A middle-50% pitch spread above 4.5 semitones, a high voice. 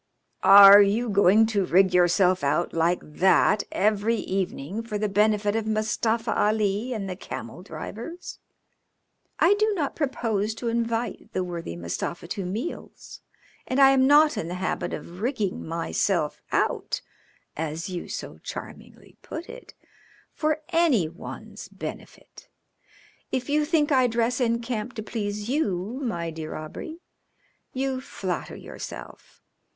Yes: average, 5.3 semitones; high, 215 Hz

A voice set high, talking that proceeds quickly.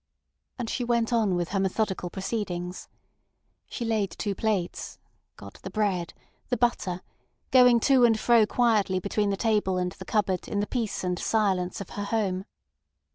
No: high, 205 Hz; average, 165 wpm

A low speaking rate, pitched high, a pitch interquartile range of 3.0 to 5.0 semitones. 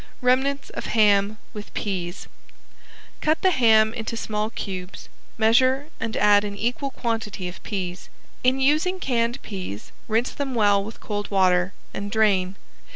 No: average, 145 wpm; high, 220 Hz; average, 3.9 semitones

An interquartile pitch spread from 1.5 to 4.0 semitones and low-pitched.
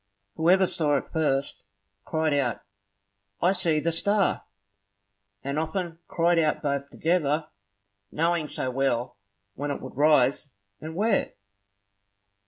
No: average, 3.3 semitones; medium, 155 Hz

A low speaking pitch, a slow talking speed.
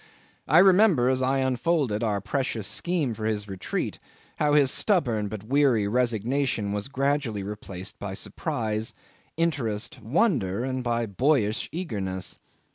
Yes: low, 120 Hz; slow, 130 wpm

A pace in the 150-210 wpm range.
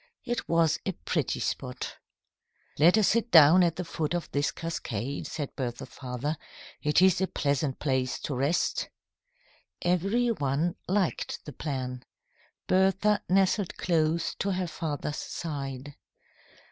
No: slow, 135 wpm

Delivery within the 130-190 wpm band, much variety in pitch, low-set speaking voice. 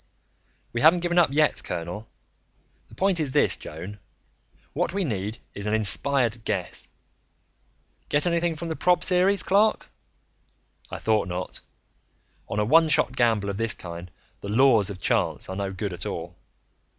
Yes: average, 160 wpm; wide, 8.6 semitones; low, 115 Hz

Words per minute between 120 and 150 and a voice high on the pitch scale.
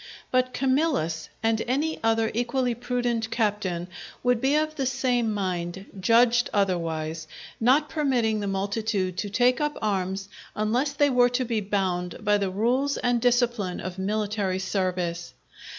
Yes: average, 145 wpm; high, 225 Hz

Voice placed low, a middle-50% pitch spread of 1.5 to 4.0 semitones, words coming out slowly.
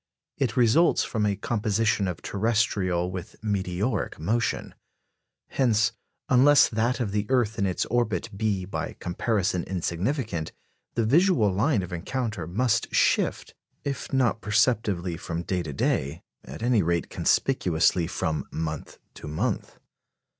No: low, 105 Hz; average, 4.9 semitones; slow, 130 wpm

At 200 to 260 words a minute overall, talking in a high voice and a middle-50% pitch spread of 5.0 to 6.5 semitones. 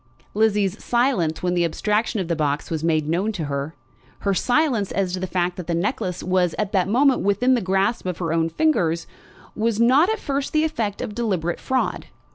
Yes: fast, 205 wpm; high, 195 Hz; wide, 5.5 semitones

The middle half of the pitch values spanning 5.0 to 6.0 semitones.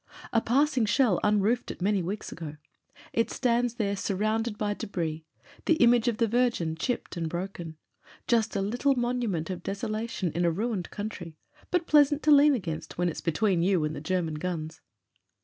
Yes: wide, 5.5 semitones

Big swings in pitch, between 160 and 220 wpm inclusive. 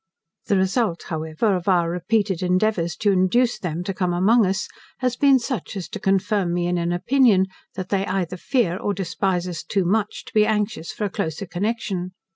No: average, 3.2 semitones; average, 195 wpm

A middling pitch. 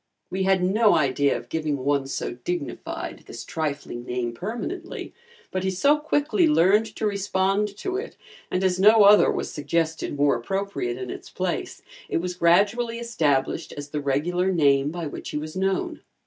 Yes: medium, 180 Hz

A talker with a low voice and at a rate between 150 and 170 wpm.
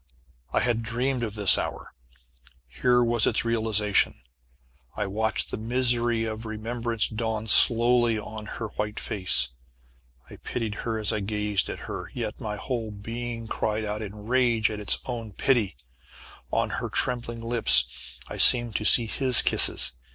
Yes: low, 110 Hz; average, 155 wpm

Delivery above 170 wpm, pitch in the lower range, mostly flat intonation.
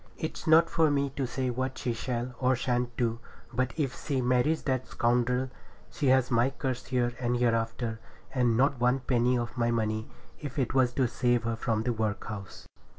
Yes: average, 190 wpm; low, 125 Hz; narrow, 1.9 semitones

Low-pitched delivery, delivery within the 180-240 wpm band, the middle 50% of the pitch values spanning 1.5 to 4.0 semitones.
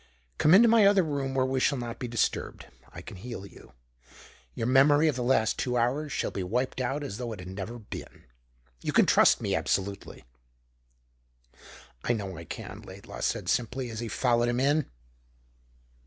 Yes: low, 125 Hz; average, 185 wpm; average, 3.4 semitones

